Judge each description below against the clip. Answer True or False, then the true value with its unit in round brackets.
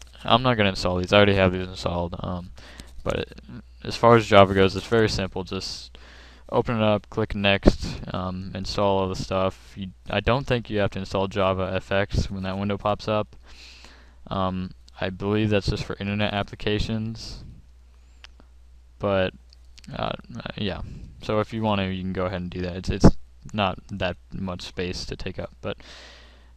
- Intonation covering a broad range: True (7.1 semitones)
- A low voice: True (95 Hz)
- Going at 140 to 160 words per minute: False (185 wpm)